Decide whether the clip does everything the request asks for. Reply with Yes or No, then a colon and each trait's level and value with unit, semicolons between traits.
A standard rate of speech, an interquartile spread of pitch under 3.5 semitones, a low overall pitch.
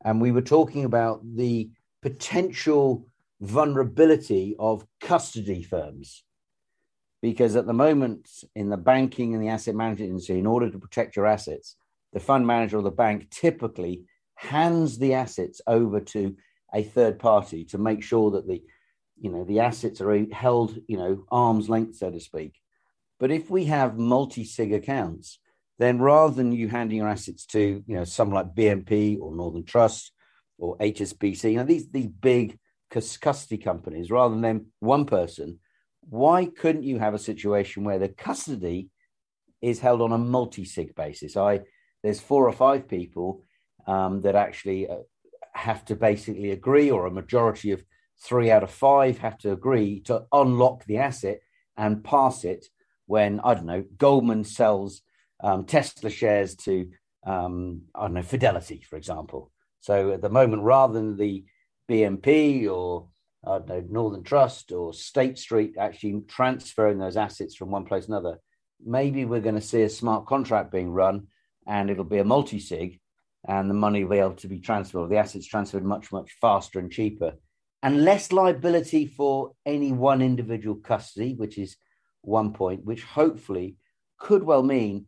No: average, 170 wpm; average, 4.4 semitones; low, 110 Hz